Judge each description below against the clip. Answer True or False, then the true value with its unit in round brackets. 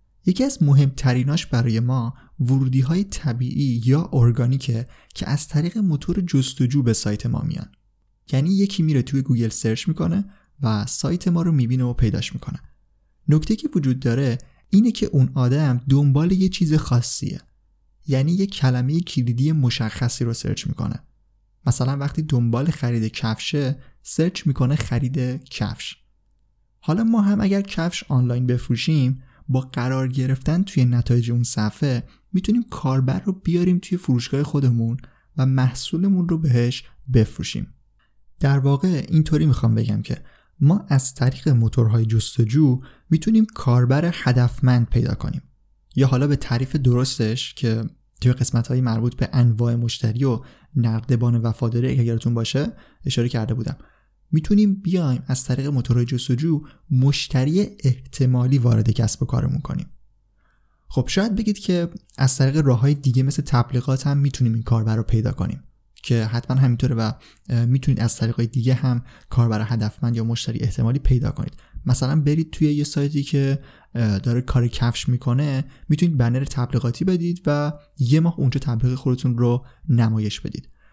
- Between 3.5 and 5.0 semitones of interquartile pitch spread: True (3.8 semitones)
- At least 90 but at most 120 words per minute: False (145 wpm)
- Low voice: True (130 Hz)